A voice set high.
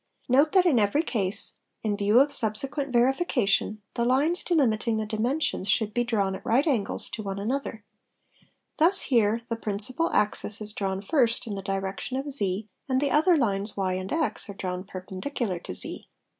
Yes: high, 220 Hz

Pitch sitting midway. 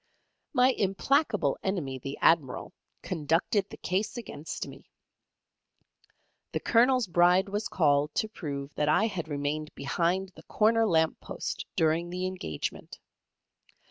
Yes: medium, 175 Hz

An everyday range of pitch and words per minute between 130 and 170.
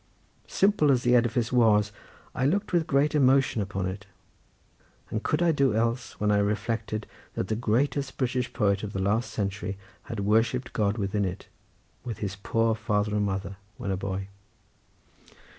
Yes: average, 3.9 semitones; average, 165 wpm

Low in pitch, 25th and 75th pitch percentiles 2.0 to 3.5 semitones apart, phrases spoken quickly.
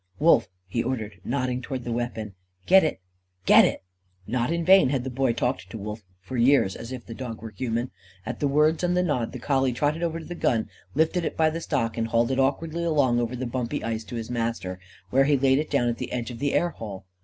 No: low, 125 Hz; average, 4.1 semitones; fast, 245 wpm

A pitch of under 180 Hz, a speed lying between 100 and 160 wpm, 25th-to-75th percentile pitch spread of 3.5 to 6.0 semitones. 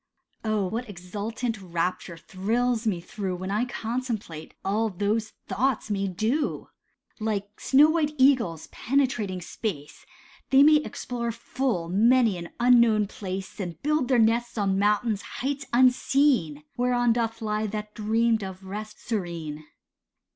No: high, 220 Hz; slow, 135 wpm; average, 4.1 semitones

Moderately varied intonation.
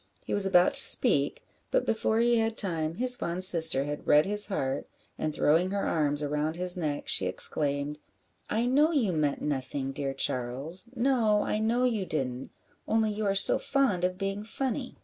No: wide, 7.0 semitones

